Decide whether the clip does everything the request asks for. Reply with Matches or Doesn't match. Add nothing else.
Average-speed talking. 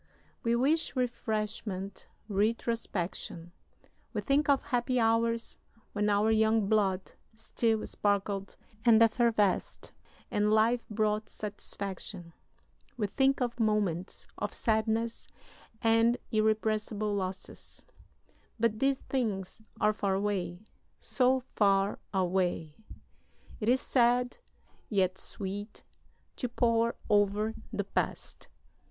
Doesn't match